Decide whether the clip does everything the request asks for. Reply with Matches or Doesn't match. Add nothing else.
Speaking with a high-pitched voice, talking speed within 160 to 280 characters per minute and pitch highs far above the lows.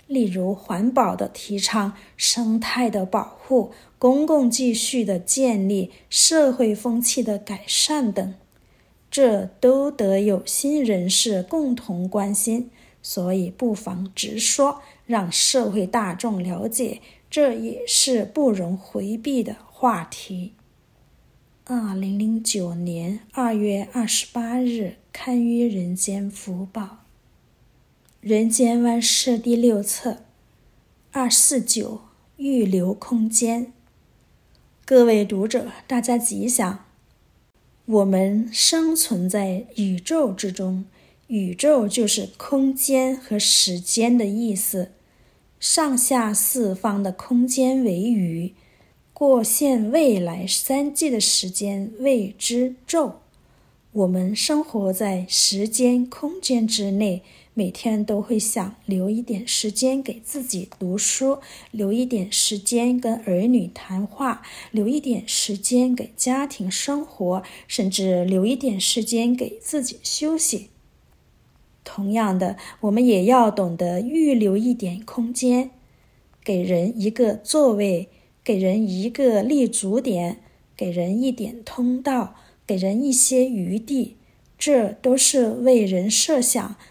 Doesn't match